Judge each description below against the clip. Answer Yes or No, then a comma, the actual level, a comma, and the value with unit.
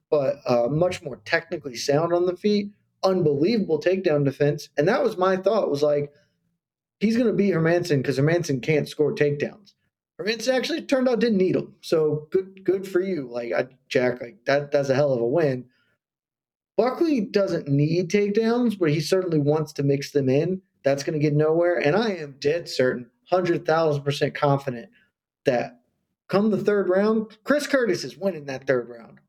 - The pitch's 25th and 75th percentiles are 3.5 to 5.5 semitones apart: Yes, average, 5.1 semitones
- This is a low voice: No, medium, 165 Hz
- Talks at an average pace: Yes, average, 185 wpm